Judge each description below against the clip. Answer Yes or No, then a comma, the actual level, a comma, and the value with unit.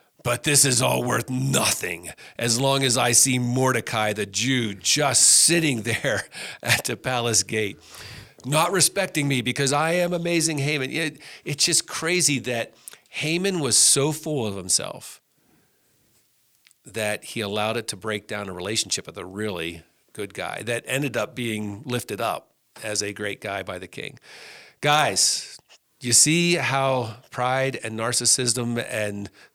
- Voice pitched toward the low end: Yes, low, 125 Hz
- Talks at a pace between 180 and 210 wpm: No, average, 150 wpm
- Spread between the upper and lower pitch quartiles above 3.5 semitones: Yes, average, 4.8 semitones